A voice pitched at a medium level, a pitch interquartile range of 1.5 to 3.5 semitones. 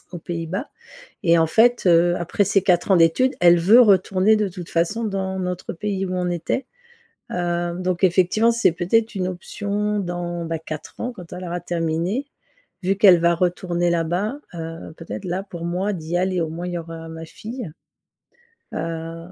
Yes: medium, 175 Hz; average, 2.7 semitones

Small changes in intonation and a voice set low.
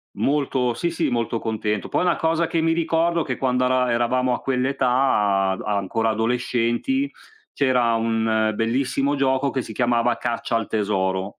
No: average, 3.3 semitones; low, 125 Hz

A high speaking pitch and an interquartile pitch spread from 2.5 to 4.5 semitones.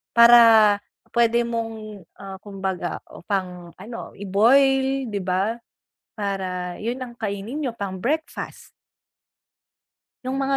Yes: high, 215 Hz; average, 3.7 semitones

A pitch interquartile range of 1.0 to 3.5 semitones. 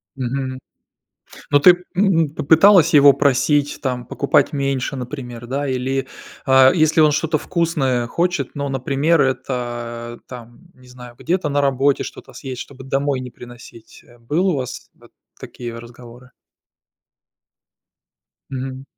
Yes: average, 2.9 semitones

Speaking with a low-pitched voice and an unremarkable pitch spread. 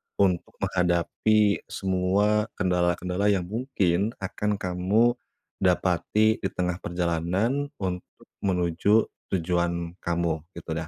Yes: very low, 90 Hz; average, 3.0 semitones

